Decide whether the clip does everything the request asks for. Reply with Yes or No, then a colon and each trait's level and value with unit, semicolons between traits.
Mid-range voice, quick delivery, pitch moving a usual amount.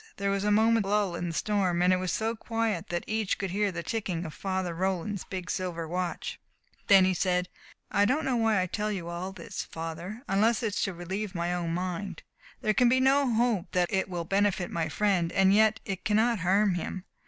No: high, 195 Hz; fast, 220 wpm; average, 3.2 semitones